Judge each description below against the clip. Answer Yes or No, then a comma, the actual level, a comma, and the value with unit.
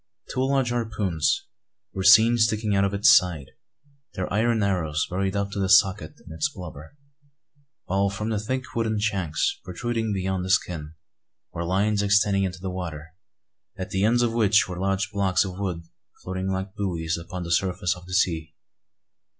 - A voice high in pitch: No, very low, 95 Hz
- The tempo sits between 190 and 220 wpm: No, average, 175 wpm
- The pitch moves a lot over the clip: No, average, 2.7 semitones